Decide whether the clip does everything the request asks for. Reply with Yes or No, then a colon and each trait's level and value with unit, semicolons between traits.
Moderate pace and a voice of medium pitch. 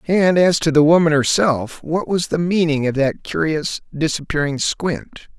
Yes: average, 165 wpm; medium, 155 Hz